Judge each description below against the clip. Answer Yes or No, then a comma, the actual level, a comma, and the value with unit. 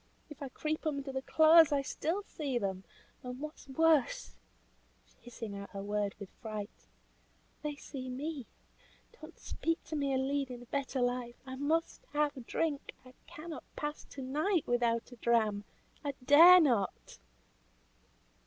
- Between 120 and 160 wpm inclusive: Yes, average, 155 wpm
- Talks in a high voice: Yes, very high, 270 Hz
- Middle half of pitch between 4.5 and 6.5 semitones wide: No, average, 4.1 semitones